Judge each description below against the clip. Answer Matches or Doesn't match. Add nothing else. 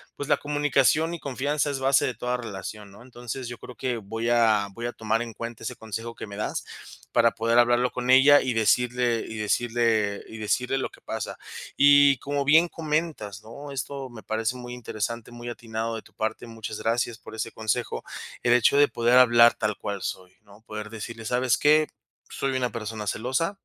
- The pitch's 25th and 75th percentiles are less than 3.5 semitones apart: Matches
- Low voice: Matches